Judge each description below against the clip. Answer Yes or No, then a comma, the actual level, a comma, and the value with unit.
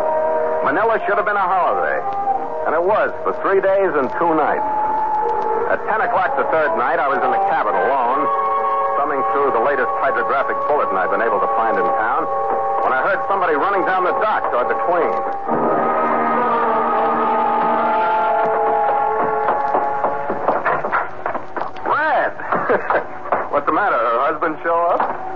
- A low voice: No, medium, 185 Hz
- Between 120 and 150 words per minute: Yes, slow, 135 wpm